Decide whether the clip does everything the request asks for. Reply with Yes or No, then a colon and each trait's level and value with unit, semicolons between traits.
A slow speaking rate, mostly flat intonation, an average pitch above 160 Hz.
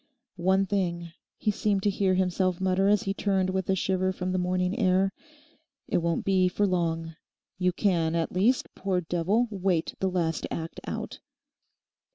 No: average, 170 wpm; narrow, 1.7 semitones; medium, 185 Hz